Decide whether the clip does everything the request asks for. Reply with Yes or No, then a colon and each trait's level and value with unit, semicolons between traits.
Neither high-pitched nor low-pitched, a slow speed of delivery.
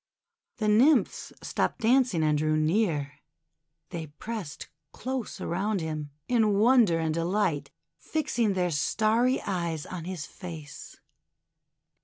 Yes: medium, 180 Hz; slow, 120 wpm